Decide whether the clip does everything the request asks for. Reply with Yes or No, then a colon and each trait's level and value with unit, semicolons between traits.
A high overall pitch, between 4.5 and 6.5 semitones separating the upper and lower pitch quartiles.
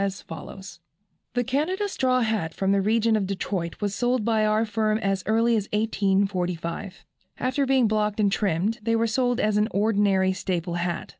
No: high, 210 Hz; average, 2.9 semitones